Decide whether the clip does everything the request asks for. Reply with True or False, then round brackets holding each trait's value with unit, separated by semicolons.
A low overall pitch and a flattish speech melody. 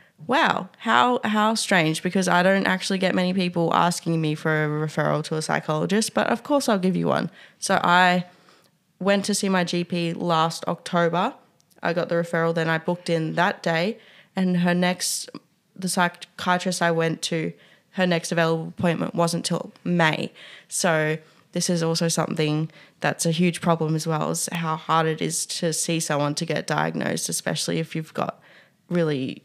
False (170 Hz; 2.2 semitones)